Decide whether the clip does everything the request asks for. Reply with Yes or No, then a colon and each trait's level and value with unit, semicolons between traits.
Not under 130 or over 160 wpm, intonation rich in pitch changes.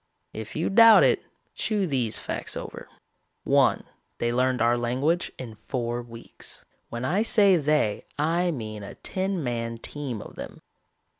Yes: average, 150 wpm; wide, 6.6 semitones